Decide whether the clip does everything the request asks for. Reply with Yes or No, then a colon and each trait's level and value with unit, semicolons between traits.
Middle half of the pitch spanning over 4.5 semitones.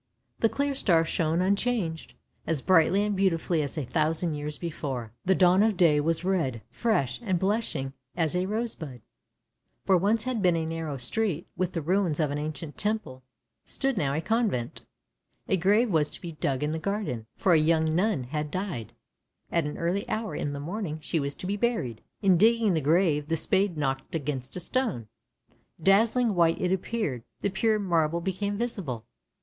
Yes: average, 5.1 semitones